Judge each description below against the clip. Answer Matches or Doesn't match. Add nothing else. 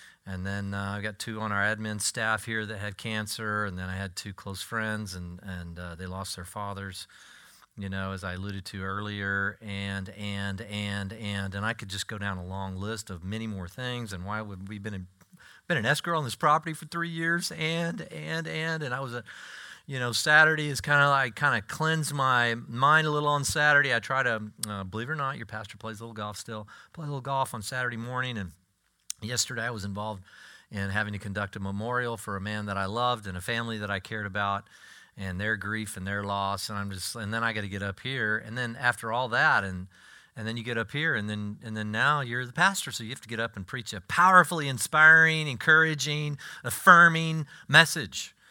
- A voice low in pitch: Matches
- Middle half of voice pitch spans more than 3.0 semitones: Matches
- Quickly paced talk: Matches